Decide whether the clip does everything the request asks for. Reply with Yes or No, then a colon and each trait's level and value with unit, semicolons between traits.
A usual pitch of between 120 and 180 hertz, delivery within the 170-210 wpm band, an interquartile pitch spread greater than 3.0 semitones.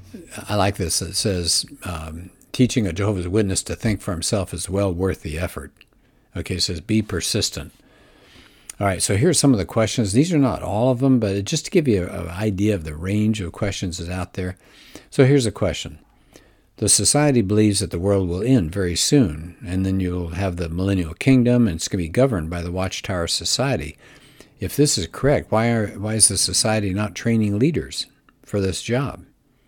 No: low, 100 Hz; average, 200 wpm; average, 3.6 semitones